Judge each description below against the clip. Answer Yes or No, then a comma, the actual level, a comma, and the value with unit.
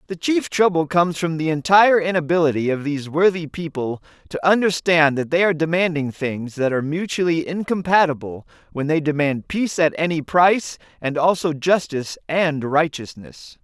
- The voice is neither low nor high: Yes, medium, 160 Hz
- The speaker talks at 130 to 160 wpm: Yes, average, 155 wpm